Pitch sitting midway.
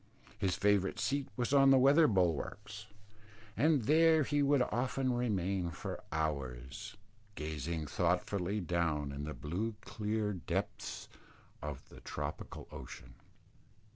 No: low, 100 Hz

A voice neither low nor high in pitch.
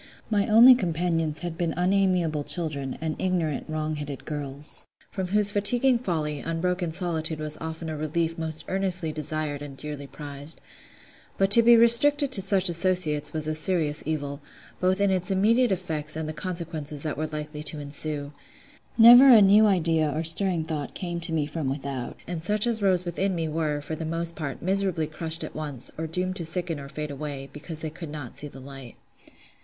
Yes: medium, 160 Hz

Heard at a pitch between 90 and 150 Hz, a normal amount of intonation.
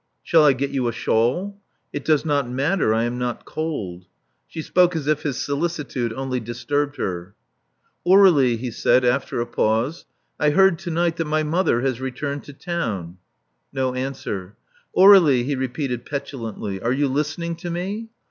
Yes: medium, 140 Hz; average, 5.0 semitones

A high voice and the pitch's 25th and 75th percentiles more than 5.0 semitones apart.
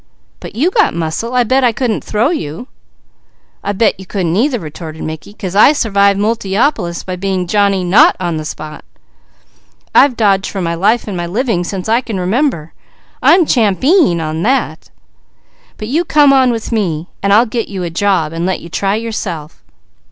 Yes: high, 200 Hz; wide, 5.4 semitones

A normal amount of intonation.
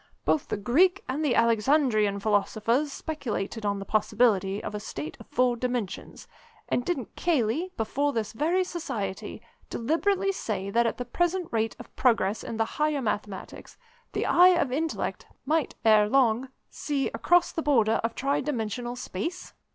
No: wide, 5.8 semitones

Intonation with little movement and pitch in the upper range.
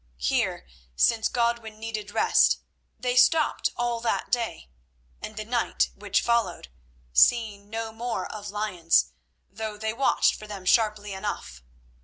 Yes: narrow, 2.3 semitones; high, 220 Hz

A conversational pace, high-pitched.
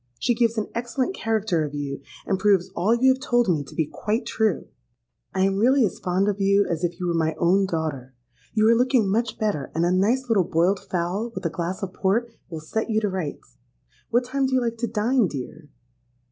No: fast, 225 wpm; high, 200 Hz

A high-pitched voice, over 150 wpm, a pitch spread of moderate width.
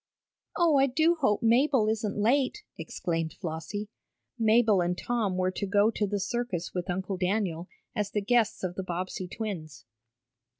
Yes: high, 205 Hz; average, 160 wpm; average, 4.3 semitones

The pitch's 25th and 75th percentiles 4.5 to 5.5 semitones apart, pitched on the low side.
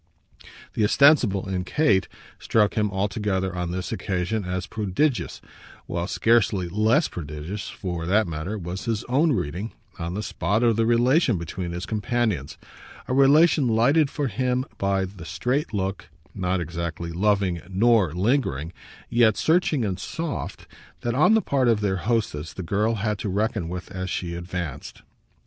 Yes: average, 4.8 semitones; low, 100 Hz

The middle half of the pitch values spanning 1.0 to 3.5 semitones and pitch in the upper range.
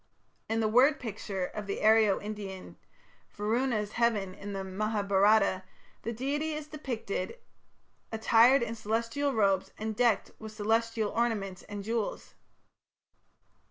Yes: narrow, 2.5 semitones; high, 220 Hz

